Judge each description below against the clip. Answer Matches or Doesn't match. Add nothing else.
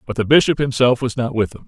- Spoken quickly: Matches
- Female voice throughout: Doesn't match